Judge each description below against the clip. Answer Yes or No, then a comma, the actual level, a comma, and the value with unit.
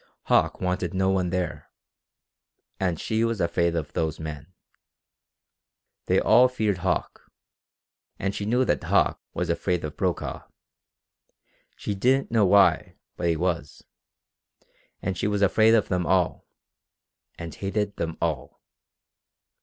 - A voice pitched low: Yes, very low, 95 Hz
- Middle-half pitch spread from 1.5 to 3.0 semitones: No, average, 3.5 semitones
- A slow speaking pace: Yes, slow, 130 wpm